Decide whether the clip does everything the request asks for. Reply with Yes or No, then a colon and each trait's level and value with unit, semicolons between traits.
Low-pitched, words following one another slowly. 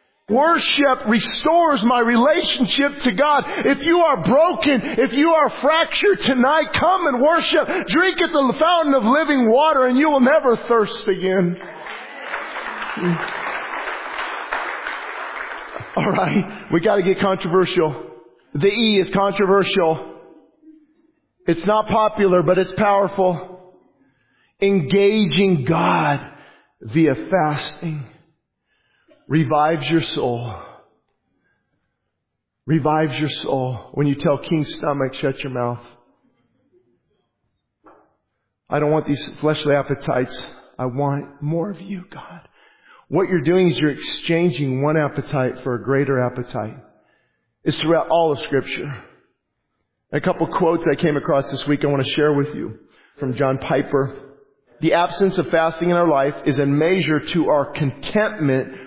No: medium, 175 Hz; slow, 125 wpm